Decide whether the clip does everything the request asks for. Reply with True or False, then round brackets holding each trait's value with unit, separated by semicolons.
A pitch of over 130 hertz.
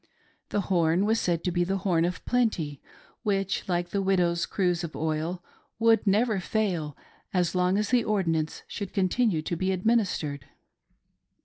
True (185 Hz)